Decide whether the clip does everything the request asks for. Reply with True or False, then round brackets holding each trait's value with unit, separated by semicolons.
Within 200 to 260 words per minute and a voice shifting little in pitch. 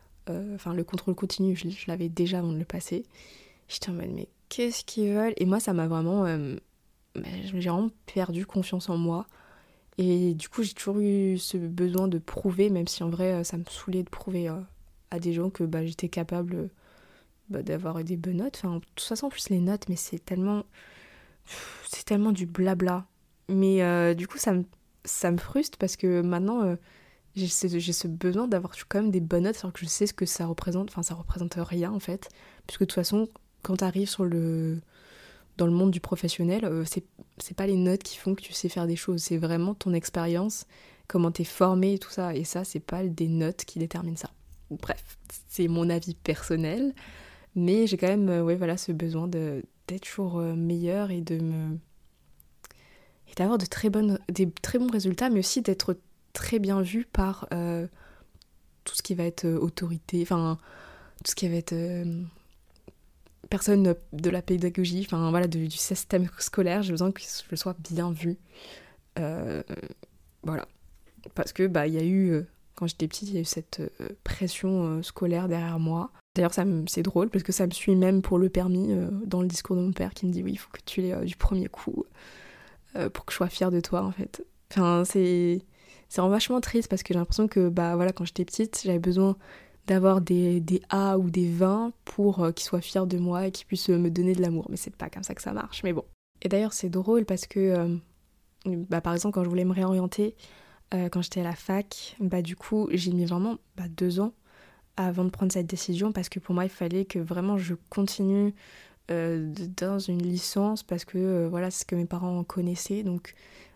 True (215 wpm; 2.0 semitones)